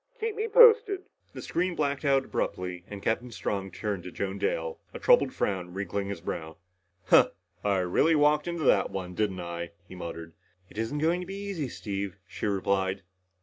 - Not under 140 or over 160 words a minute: No, average, 185 wpm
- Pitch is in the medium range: No, low, 105 Hz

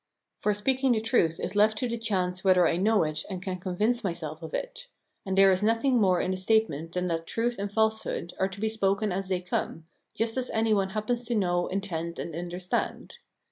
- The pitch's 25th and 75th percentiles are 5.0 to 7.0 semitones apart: No, average, 3.7 semitones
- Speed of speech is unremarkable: No, fast, 220 wpm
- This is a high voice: Yes, high, 195 Hz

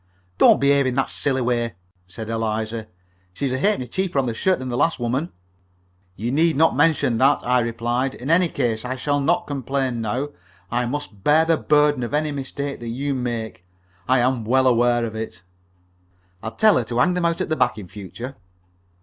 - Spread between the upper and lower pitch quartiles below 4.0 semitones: Yes, average, 3.5 semitones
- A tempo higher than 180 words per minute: Yes, average, 200 wpm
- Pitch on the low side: Yes, low, 130 Hz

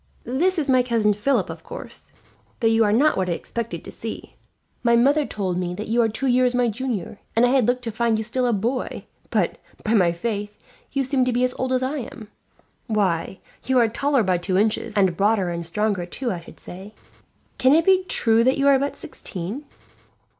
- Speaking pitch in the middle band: No, high, 230 Hz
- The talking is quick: Yes, fast, 220 wpm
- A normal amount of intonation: Yes, average, 4.1 semitones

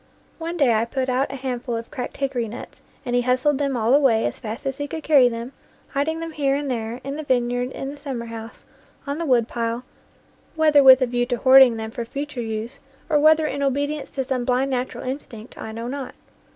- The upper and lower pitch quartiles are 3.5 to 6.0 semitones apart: No, average, 2.9 semitones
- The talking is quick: Yes, fast, 220 wpm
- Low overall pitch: No, very high, 260 Hz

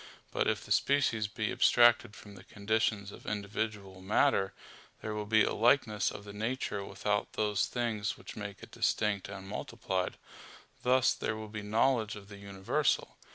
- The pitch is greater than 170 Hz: No, low, 105 Hz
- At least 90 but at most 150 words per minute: No, average, 165 wpm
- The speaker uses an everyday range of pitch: No, narrow, 1.8 semitones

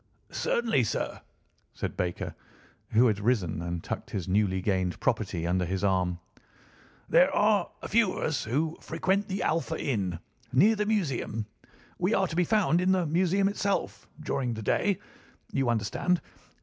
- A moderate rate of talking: Yes, average, 155 wpm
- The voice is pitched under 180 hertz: Yes, low, 135 Hz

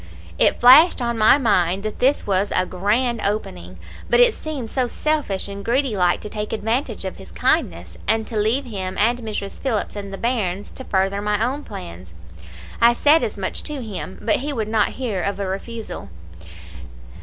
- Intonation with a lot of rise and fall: No, average, 3.7 semitones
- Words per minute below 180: No, average, 190 wpm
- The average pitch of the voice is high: Yes, high, 215 Hz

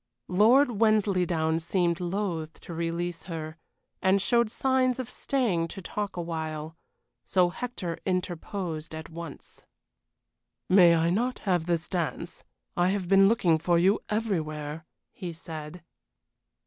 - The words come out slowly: Yes, slow, 125 wpm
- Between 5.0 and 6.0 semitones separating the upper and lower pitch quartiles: No, average, 3.6 semitones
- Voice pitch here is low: No, medium, 175 Hz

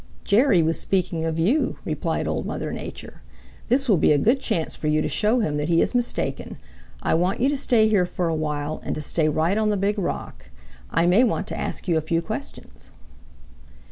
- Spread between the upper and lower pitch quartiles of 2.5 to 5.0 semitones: No, wide, 5.5 semitones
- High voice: No, medium, 175 Hz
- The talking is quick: Yes, fast, 215 wpm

